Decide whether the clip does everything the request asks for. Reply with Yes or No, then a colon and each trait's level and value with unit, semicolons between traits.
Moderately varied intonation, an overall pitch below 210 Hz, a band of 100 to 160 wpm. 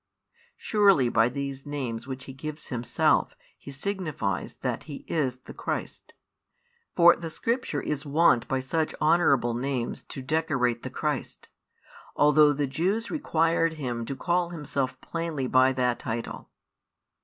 Yes: average, 4.1 semitones; medium, 140 Hz; average, 140 wpm